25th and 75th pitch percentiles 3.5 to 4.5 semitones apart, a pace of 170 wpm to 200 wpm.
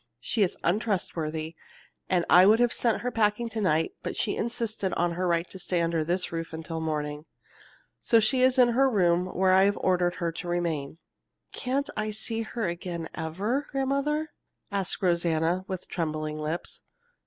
No: average, 5.2 semitones; average, 175 wpm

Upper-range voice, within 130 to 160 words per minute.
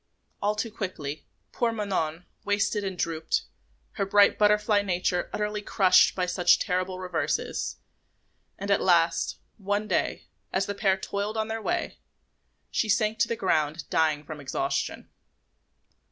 Yes: high, 195 Hz; average, 140 wpm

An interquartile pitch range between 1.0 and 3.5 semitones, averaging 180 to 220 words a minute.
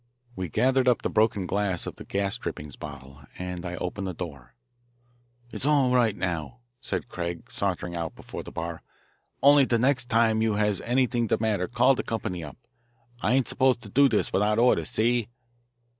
No: wide, 5.6 semitones; average, 185 wpm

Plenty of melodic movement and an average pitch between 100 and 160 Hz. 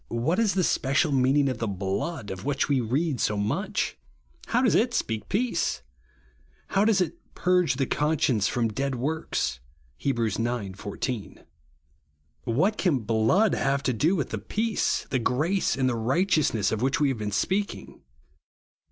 Yes: wide, 7.1 semitones; low, 135 Hz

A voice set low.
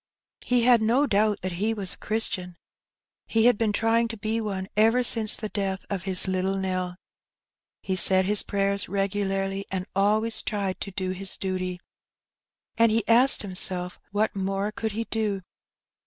No: high, 200 Hz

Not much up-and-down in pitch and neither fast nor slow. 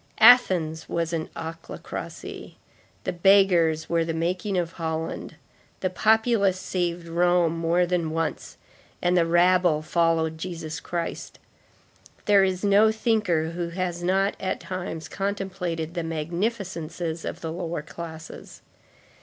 No: narrow, 2.3 semitones; slow, 125 wpm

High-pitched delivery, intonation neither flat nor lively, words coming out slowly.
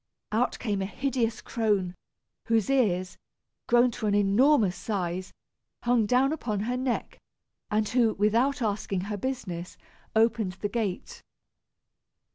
Yes: high, 220 Hz; average, 3.6 semitones; slow, 125 wpm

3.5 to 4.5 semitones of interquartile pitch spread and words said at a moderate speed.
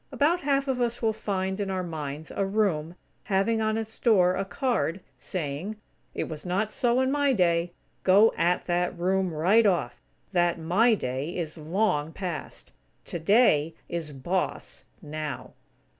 No: average, 5.1 semitones; average, 155 wpm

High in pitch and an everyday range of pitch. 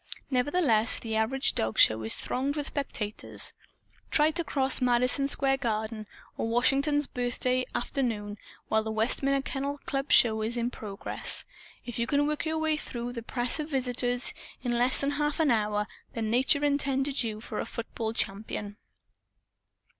Yes: high, 245 Hz; average, 4.0 semitones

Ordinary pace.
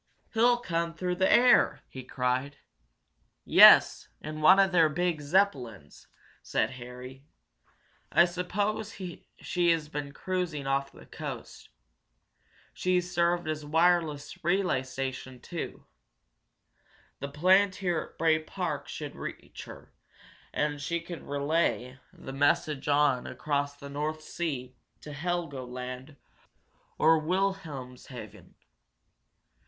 No: slow, 115 wpm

